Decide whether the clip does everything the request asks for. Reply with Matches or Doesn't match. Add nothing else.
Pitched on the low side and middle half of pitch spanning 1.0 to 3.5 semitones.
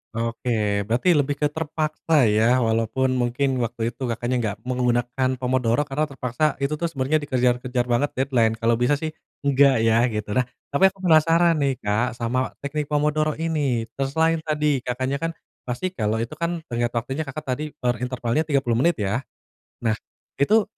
Doesn't match